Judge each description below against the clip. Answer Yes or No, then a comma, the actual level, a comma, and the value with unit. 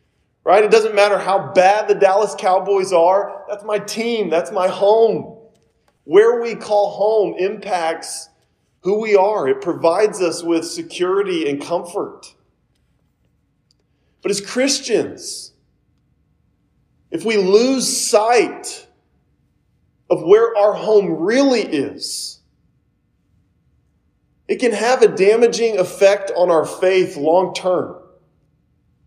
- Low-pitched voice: No, high, 205 Hz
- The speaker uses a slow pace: Yes, slow, 115 wpm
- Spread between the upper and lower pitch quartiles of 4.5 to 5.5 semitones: No, average, 3.4 semitones